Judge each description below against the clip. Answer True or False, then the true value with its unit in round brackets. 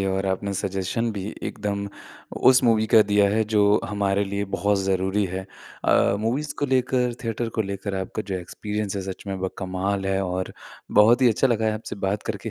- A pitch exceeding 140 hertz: False (100 Hz)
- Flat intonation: True (2.3 semitones)